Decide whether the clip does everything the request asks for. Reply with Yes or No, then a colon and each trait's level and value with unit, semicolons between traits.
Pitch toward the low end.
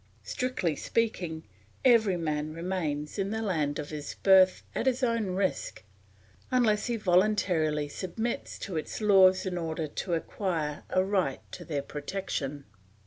No: medium, 185 Hz